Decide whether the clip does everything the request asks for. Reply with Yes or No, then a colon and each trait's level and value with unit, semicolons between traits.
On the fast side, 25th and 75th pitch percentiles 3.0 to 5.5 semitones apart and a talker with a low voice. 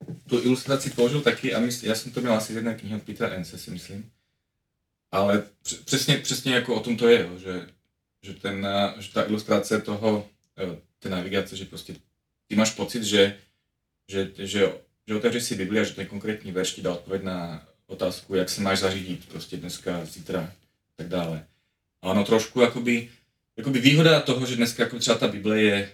Yes: fast, 185 wpm; average, 4.0 semitones; low, 105 Hz